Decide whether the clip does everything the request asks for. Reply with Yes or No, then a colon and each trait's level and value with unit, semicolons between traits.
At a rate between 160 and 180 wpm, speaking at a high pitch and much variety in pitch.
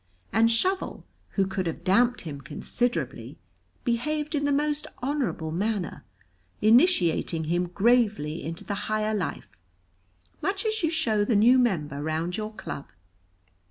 No: slow, 135 wpm; high, 215 Hz; wide, 7.0 semitones